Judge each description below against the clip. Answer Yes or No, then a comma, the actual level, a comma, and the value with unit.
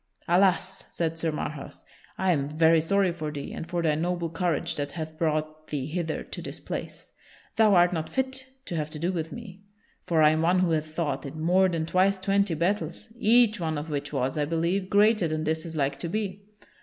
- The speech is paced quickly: Yes, fast, 215 wpm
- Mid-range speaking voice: Yes, medium, 165 Hz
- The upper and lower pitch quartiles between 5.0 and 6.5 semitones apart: No, average, 3.1 semitones